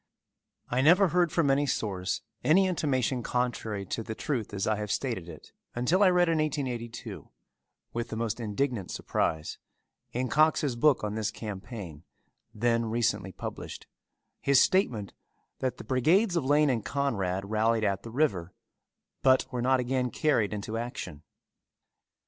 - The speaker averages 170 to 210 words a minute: No, average, 150 wpm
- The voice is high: No, low, 120 Hz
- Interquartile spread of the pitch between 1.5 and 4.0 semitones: No, average, 4.9 semitones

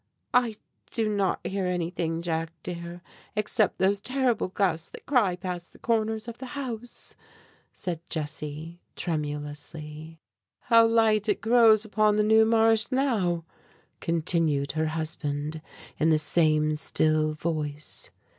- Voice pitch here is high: No, medium, 175 Hz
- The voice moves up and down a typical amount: No, wide, 5.8 semitones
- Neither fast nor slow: No, slow, 125 wpm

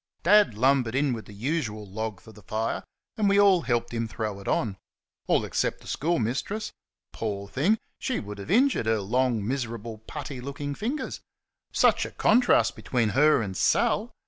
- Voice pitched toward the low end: Yes, low, 120 Hz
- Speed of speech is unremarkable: Yes, average, 170 wpm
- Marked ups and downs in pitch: Yes, wide, 6.1 semitones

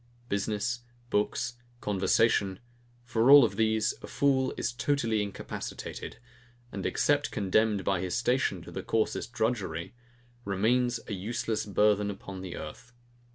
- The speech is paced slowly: Yes, slow, 130 wpm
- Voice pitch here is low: Yes, low, 110 Hz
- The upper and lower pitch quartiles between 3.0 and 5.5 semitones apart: Yes, average, 3.4 semitones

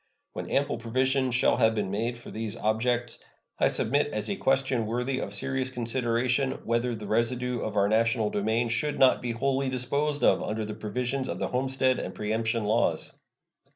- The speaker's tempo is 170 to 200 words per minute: Yes, average, 175 wpm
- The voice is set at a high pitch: No, low, 120 Hz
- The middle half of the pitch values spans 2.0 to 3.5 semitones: Yes, average, 2.8 semitones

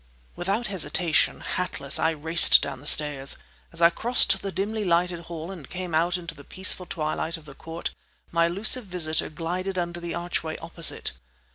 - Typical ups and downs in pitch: No, narrow, 2.3 semitones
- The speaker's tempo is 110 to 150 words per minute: No, average, 170 wpm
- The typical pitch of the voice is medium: Yes, medium, 170 Hz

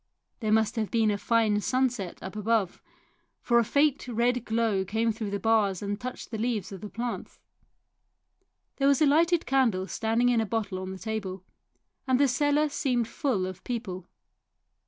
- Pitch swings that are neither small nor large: Yes, average, 3.4 semitones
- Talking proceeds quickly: No, average, 175 wpm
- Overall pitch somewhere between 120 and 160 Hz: No, high, 225 Hz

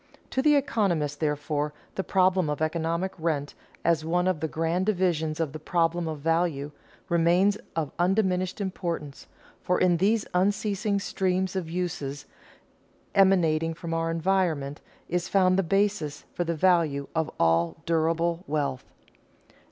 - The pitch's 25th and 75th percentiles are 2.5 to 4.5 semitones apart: Yes, average, 3.1 semitones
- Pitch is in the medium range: Yes, medium, 170 Hz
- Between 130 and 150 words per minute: Yes, average, 140 wpm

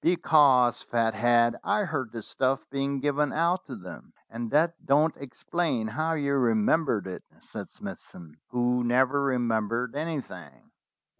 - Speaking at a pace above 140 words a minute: No, slow, 135 wpm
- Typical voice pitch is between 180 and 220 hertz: No, low, 130 Hz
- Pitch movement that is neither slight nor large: Yes, average, 4.2 semitones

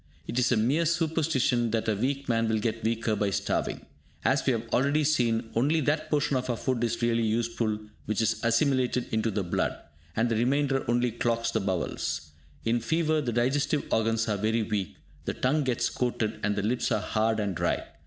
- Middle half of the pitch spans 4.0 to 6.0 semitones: No, average, 3.2 semitones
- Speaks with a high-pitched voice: No, low, 115 Hz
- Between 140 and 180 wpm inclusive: No, average, 200 wpm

